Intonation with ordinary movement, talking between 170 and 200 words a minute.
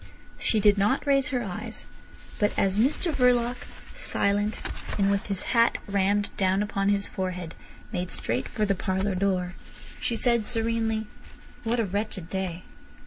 No: average, 3.1 semitones; average, 150 wpm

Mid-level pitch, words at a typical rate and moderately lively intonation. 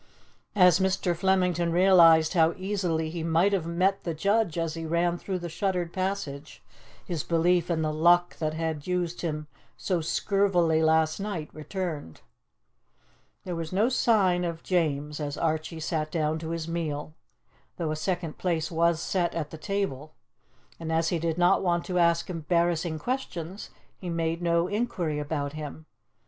No: medium, 170 Hz; average, 160 wpm; narrow, 2.3 semitones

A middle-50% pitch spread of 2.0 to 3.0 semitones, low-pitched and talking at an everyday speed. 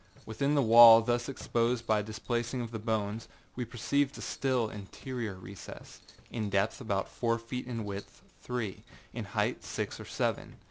Yes: narrow, 2.6 semitones; low, 115 Hz; average, 170 wpm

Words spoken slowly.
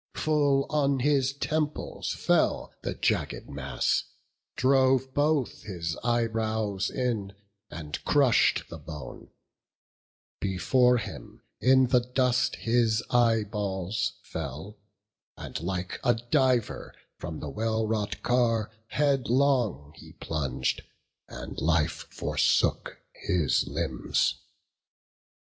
Yes: slow, 100 wpm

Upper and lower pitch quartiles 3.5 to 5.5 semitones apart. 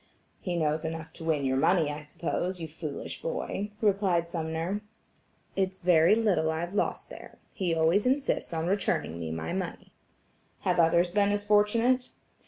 Yes: average, 4.1 semitones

